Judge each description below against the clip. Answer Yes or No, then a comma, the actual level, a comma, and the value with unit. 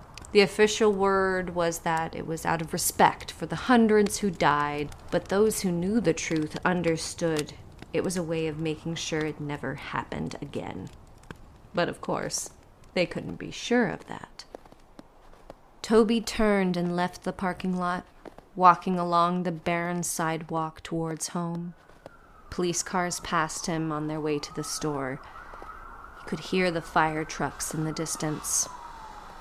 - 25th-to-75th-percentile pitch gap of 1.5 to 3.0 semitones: Yes, narrow, 2.6 semitones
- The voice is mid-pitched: Yes, medium, 170 Hz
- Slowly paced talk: No, average, 155 wpm